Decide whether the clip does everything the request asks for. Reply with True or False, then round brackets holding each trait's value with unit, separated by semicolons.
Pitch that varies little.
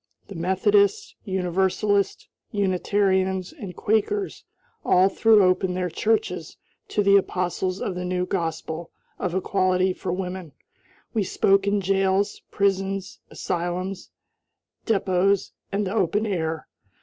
True (1.7 semitones)